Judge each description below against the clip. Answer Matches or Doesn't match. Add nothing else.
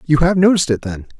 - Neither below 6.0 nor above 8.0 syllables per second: Matches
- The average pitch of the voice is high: Doesn't match